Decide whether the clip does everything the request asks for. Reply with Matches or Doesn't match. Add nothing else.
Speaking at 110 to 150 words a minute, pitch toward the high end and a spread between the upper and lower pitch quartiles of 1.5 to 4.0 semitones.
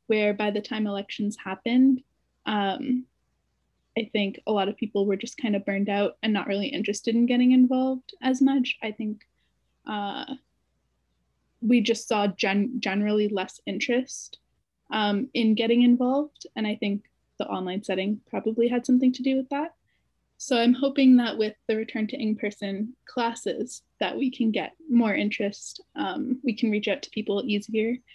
Doesn't match